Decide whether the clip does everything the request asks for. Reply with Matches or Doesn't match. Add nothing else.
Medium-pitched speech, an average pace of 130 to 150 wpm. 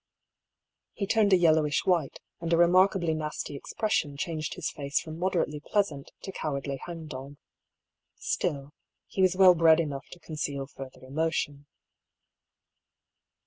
Matches